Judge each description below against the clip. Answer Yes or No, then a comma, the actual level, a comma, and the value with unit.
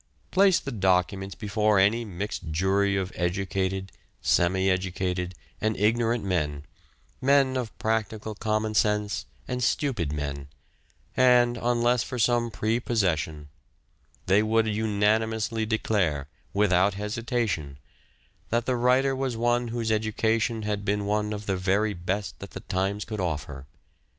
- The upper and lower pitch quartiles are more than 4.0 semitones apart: No, average, 3.5 semitones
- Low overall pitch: Yes, low, 105 Hz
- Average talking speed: No, slow, 125 wpm